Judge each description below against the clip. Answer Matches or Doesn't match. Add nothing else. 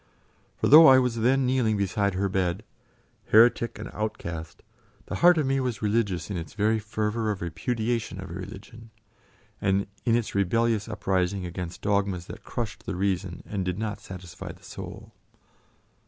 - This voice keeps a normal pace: Matches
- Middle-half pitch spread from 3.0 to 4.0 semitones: Matches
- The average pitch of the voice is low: Matches